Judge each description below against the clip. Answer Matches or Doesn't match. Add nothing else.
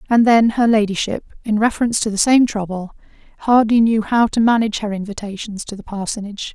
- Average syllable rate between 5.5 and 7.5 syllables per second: Matches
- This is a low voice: Doesn't match